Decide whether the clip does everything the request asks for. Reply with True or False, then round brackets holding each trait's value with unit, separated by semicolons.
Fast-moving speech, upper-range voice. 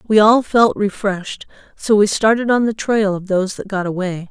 True (210 wpm; 205 Hz)